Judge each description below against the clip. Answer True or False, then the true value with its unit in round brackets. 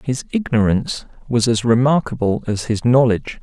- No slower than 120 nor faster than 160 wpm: True (140 wpm)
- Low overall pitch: True (120 Hz)